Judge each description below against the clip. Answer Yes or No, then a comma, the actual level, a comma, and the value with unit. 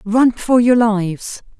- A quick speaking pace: No, average, 150 wpm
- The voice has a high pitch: Yes, high, 225 Hz